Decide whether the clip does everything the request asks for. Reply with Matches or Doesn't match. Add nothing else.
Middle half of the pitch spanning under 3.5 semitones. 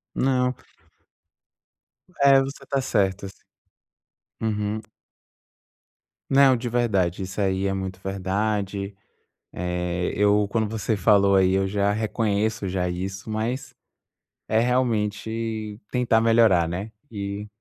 Matches